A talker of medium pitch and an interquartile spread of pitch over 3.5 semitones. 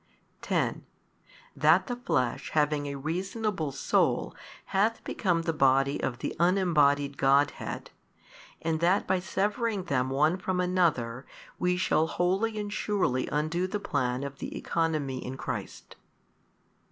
Yes: medium, 160 Hz; average, 5.0 semitones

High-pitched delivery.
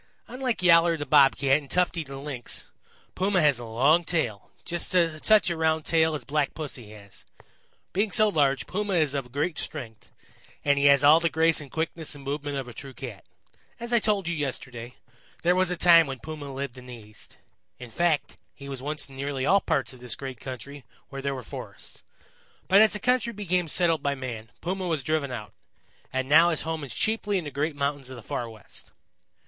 No: medium, 145 Hz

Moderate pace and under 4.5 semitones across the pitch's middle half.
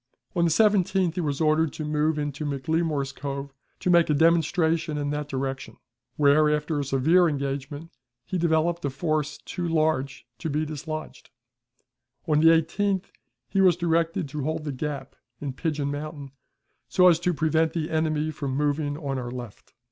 Yes: average, 170 wpm; narrow, 2.4 semitones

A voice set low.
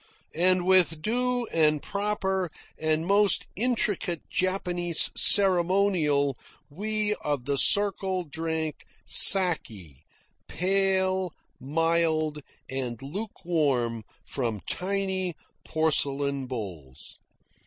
No: medium, 170 Hz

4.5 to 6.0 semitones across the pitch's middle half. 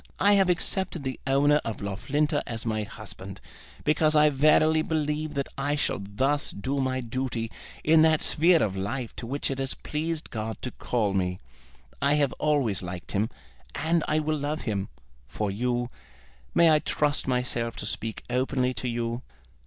Yes: average, 5.0 semitones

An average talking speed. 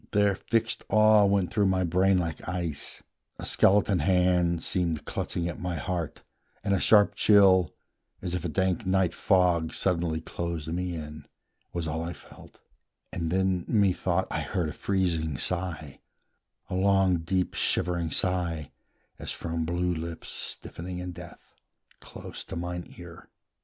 Yes: average, 150 wpm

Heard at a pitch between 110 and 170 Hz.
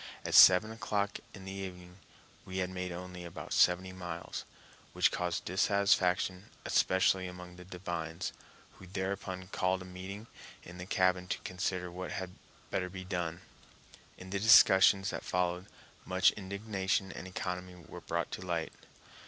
No: very low, 90 Hz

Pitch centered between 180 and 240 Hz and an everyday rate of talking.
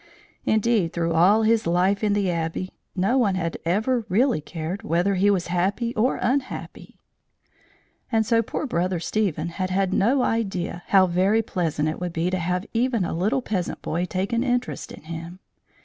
Yes: high, 190 Hz; average, 180 wpm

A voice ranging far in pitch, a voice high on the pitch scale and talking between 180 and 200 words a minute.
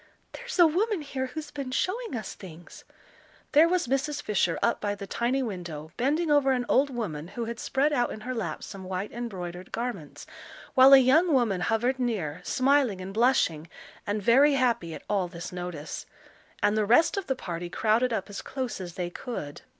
Yes: wide, 6.6 semitones; high, 235 Hz; average, 190 wpm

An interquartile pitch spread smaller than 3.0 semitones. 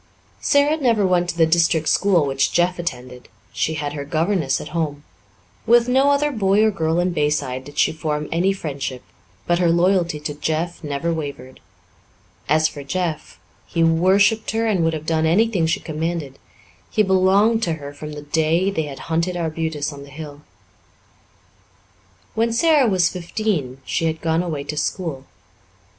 No: average, 4.0 semitones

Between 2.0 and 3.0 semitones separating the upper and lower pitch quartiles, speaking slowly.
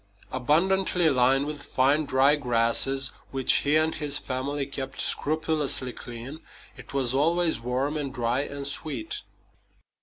Yes: average, 2.7 semitones; slow, 130 wpm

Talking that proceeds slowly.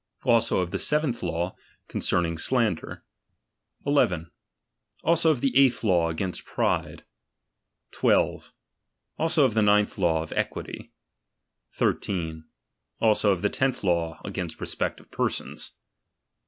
Yes: slow, 120 wpm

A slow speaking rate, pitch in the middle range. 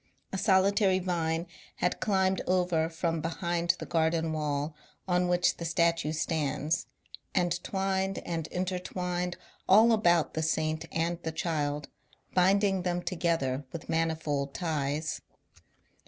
Yes: slow, 125 wpm; medium, 170 Hz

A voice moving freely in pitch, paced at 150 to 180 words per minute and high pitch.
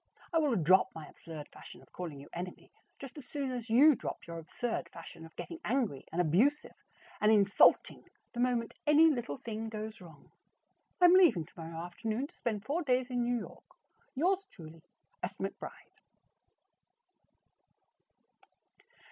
Yes: wide, 7.4 semitones; average, 155 wpm; high, 220 Hz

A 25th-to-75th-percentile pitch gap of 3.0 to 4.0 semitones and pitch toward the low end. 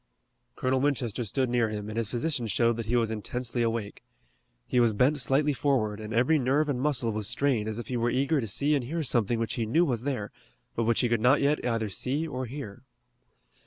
Yes: average, 3.4 semitones; low, 120 Hz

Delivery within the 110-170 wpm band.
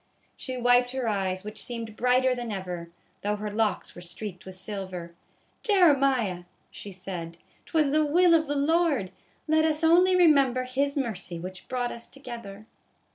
Yes: average, 160 wpm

